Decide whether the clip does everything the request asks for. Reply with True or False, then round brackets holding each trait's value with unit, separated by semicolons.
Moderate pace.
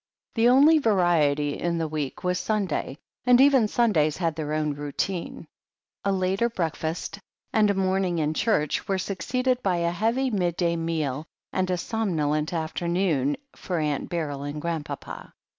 True (150 wpm)